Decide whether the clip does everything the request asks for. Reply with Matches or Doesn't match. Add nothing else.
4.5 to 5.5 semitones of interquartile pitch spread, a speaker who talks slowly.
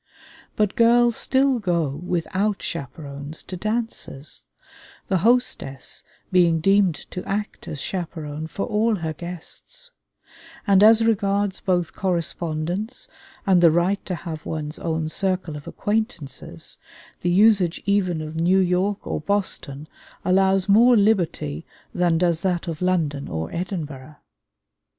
Doesn't match